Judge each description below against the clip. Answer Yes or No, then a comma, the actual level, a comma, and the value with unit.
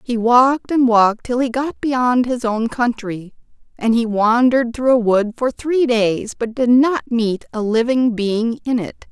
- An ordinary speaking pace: Yes, average, 190 wpm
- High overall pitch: Yes, high, 240 Hz